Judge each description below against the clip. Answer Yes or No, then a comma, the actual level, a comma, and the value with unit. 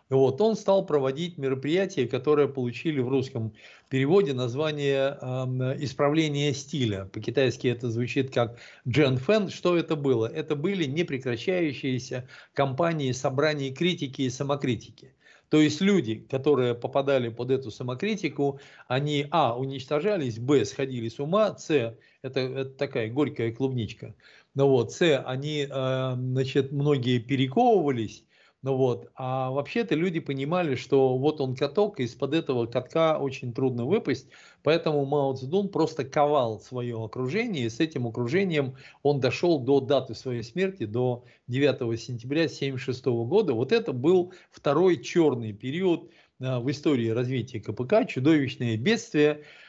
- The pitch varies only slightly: No, average, 3.2 semitones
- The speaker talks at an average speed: Yes, average, 135 wpm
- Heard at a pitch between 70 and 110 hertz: No, low, 135 Hz